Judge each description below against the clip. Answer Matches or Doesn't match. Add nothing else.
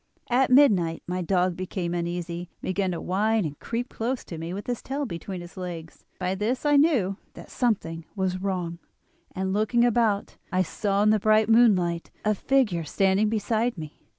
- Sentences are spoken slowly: Doesn't match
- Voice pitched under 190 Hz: Doesn't match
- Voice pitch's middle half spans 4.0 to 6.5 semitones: Matches